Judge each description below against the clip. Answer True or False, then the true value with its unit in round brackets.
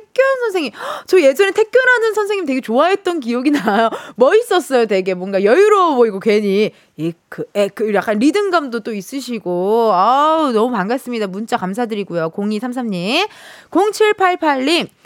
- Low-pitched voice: False (255 Hz)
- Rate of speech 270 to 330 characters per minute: True (310 characters per minute)